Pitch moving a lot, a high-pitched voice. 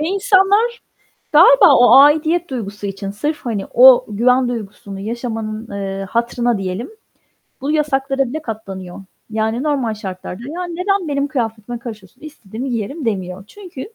Yes: wide, 6.2 semitones; high, 240 Hz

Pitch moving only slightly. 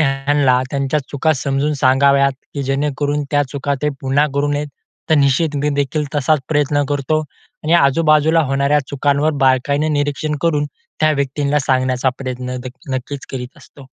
Yes: narrow, 1.6 semitones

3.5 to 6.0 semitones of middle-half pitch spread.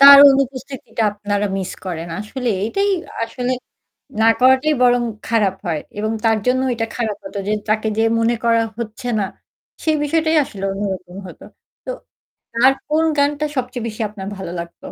Yes: average, 4.2 semitones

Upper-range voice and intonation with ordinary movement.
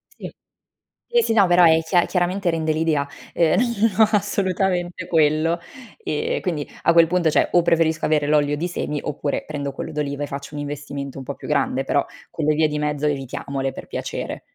No: medium, 155 Hz; average, 3.3 semitones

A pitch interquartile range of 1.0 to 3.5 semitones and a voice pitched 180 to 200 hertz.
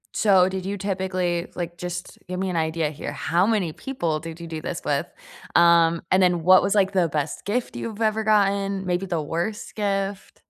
Yes: average, 2.7 semitones; medium, 185 Hz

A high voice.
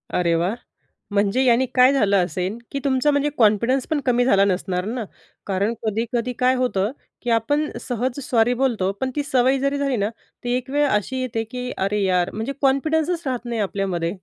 Yes: high, 240 Hz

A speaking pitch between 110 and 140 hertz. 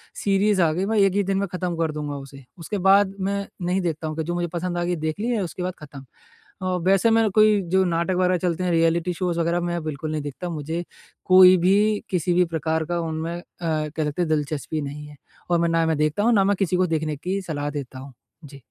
No: medium, 175 Hz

